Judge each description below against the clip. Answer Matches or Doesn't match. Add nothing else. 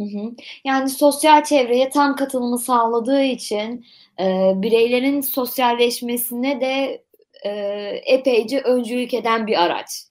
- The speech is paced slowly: Matches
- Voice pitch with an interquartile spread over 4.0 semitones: Doesn't match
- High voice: Matches